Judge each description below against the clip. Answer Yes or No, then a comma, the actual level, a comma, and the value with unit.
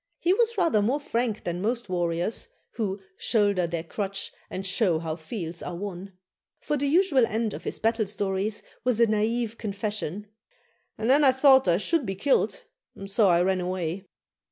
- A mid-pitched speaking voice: No, high, 205 Hz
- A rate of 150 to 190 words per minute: Yes, average, 180 wpm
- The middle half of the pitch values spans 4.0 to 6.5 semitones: Yes, average, 4.5 semitones